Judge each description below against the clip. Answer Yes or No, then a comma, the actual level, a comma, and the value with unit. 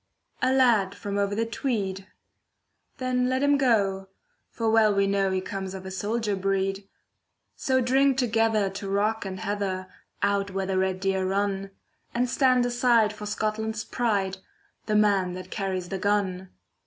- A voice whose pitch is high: Yes, high, 205 Hz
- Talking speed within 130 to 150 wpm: No, average, 160 wpm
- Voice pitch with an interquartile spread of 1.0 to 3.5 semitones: Yes, average, 2.9 semitones